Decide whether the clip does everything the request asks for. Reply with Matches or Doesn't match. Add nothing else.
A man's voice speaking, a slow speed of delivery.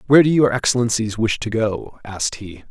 Doesn't match